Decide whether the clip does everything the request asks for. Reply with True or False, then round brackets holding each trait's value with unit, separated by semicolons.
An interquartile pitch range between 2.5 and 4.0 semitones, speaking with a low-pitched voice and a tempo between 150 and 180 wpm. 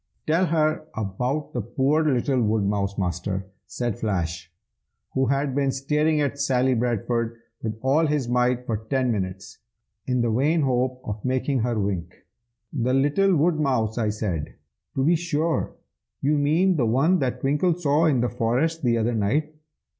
False (5.1 semitones; 130 Hz; 160 wpm)